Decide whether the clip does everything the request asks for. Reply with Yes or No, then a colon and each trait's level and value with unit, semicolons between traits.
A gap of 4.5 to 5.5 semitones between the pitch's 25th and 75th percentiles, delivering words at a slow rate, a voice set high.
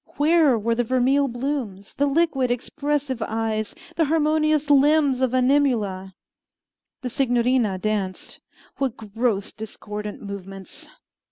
Yes: average, 4.9 semitones; slow, 110 wpm; very high, 250 Hz